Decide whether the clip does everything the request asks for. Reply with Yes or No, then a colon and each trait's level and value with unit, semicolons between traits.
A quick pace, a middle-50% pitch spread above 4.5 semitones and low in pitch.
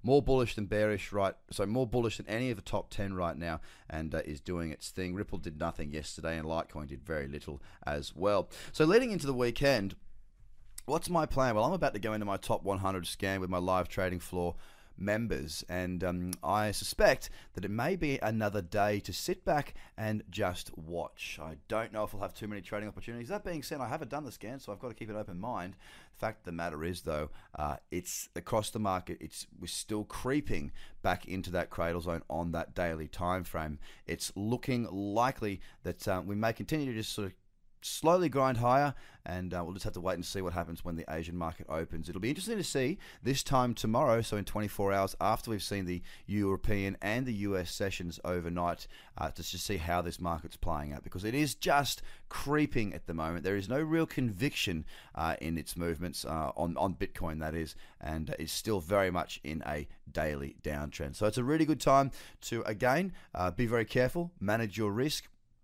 Yes: fast, 215 wpm; average, 5.0 semitones; very low, 95 Hz